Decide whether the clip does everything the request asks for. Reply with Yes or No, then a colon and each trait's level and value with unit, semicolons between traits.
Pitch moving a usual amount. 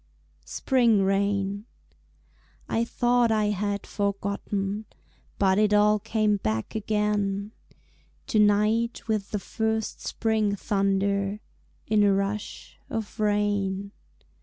No: narrow, 1.5 semitones